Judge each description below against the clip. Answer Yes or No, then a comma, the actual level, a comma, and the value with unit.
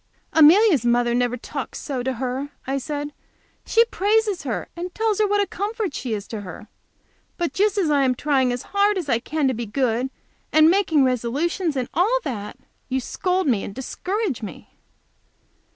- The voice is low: No, very high, 290 Hz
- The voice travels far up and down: Yes, wide, 7.4 semitones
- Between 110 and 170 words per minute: No, average, 185 wpm